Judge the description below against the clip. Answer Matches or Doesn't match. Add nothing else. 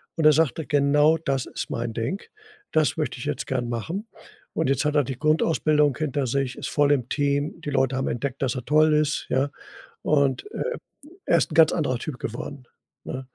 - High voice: Doesn't match